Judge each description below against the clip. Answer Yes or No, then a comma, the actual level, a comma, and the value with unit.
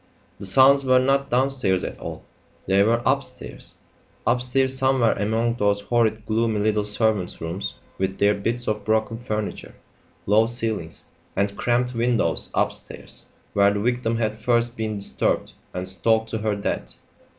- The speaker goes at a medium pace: Yes, average, 150 wpm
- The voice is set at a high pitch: No, low, 110 Hz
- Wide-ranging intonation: No, average, 3.1 semitones